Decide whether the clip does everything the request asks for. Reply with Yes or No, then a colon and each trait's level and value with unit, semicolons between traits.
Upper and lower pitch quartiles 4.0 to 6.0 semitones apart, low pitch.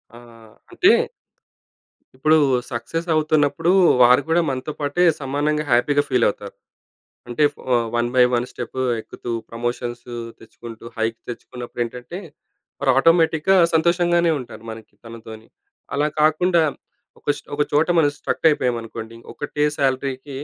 Yes: average, 4.6 semitones; low, 130 Hz